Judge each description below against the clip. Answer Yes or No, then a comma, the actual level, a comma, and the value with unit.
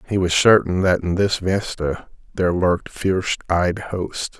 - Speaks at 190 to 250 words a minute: No, average, 165 wpm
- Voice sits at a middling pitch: No, very low, 90 Hz